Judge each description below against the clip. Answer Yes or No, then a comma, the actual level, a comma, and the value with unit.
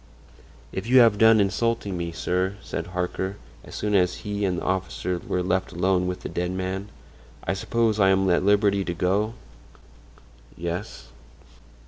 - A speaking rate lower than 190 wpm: Yes, average, 160 wpm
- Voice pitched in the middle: No, very low, 95 Hz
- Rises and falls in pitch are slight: Yes, narrow, 2.2 semitones